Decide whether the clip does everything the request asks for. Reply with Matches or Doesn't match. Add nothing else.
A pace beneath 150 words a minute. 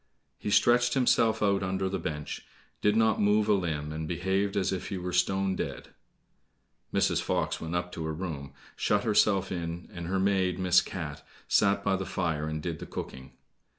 Doesn't match